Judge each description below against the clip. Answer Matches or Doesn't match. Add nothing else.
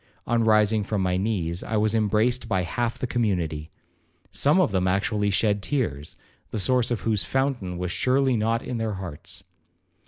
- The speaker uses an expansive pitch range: Doesn't match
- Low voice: Matches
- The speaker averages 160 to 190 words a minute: Matches